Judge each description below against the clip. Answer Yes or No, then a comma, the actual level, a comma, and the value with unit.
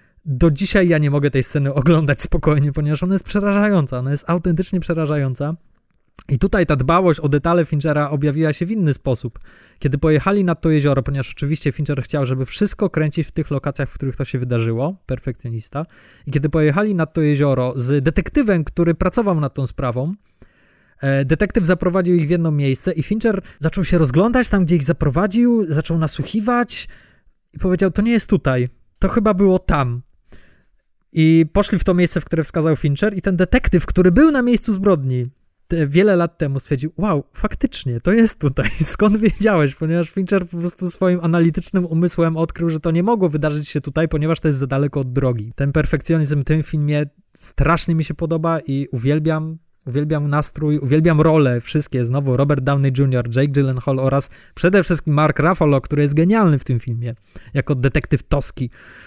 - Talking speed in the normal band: No, fast, 180 wpm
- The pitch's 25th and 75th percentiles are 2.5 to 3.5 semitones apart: No, average, 4.2 semitones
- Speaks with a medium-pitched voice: Yes, medium, 155 Hz